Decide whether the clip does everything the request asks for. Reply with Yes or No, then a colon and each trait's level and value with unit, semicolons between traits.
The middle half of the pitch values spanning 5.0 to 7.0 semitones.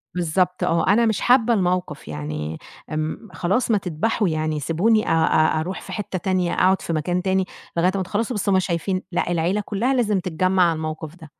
No: average, 3.7 semitones